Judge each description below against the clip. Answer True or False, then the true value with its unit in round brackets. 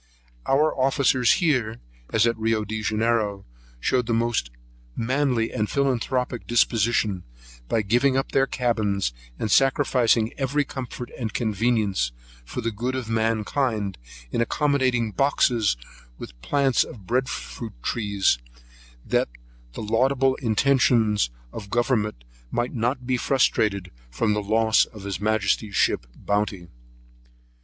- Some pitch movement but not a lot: True (3.4 semitones)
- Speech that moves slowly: True (125 wpm)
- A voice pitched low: True (115 Hz)